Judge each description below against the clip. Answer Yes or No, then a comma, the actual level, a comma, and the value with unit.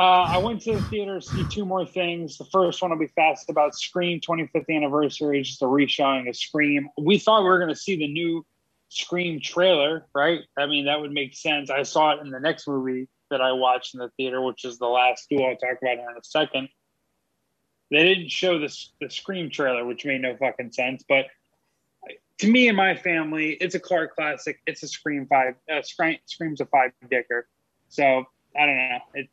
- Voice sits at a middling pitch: Yes, medium, 150 Hz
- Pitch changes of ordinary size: Yes, average, 4.4 semitones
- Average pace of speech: No, fast, 215 wpm